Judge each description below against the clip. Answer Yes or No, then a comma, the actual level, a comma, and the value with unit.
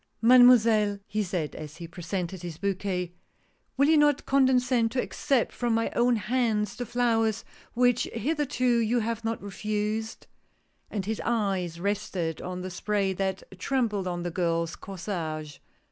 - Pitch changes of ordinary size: Yes, average, 4.8 semitones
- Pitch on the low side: No, high, 210 Hz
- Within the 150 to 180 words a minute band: Yes, average, 160 wpm